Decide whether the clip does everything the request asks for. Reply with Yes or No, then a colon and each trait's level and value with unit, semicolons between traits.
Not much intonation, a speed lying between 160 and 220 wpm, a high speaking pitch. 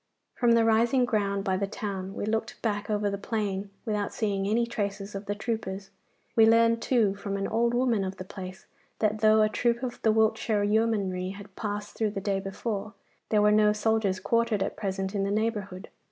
Yes: narrow, 2.1 semitones; average, 200 wpm; high, 210 Hz